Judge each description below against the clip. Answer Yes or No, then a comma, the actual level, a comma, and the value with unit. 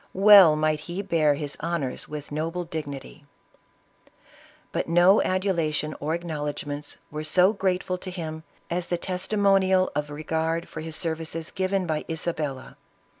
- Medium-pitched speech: Yes, medium, 165 Hz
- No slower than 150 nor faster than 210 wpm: No, average, 140 wpm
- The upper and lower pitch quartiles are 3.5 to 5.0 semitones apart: No, average, 3.1 semitones